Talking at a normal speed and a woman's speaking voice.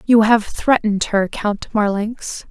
Yes: average, 145 wpm; female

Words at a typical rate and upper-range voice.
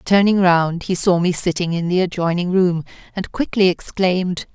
No: average, 170 wpm; medium, 180 Hz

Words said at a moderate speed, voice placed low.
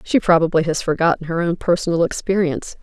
No: average, 170 wpm; medium, 170 Hz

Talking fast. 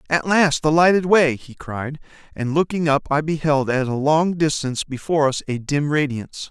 No: average, 195 wpm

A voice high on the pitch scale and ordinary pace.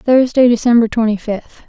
Yes: high, 230 Hz; average, 145 wpm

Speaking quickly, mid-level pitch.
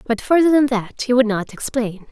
No: fast, 225 wpm; high, 240 Hz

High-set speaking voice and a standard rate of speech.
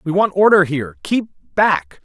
No: medium, 165 Hz; average, 145 wpm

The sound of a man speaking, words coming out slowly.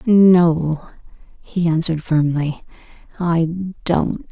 No: female; slow, 85 wpm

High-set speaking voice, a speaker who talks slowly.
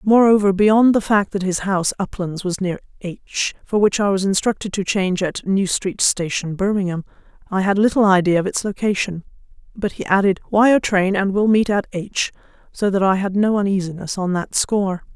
No: high, 195 Hz; average, 195 wpm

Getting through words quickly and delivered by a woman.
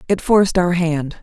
No: average, 195 wpm; female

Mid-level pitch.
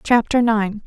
No: high, 220 Hz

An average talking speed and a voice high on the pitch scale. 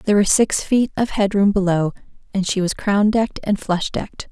No: fast, 220 wpm; high, 200 Hz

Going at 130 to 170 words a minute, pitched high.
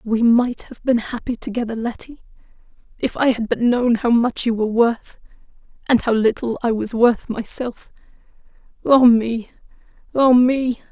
Yes: average, 150 wpm; high, 235 Hz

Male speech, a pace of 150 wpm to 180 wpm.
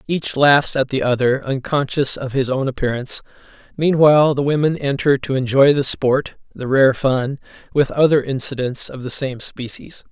Yes: male; average, 165 wpm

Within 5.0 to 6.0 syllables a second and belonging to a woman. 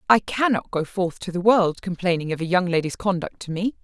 Yes: 5.5 syllables/s; female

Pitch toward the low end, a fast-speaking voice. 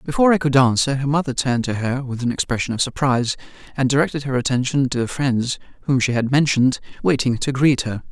Yes: low, 130 Hz; fast, 215 wpm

